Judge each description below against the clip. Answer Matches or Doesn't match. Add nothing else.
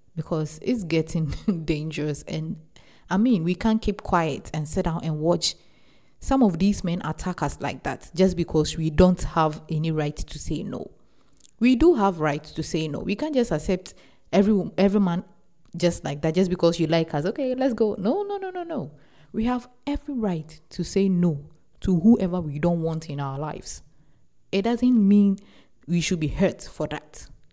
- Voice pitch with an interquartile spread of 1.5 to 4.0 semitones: Doesn't match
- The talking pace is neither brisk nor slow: Matches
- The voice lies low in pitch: Doesn't match